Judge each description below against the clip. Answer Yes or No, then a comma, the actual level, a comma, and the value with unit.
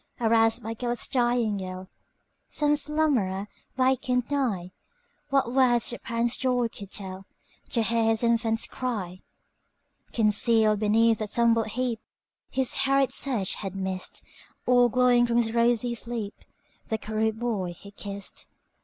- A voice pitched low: No, high, 230 Hz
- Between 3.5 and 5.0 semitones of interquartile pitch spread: No, average, 2.7 semitones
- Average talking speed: No, slow, 110 wpm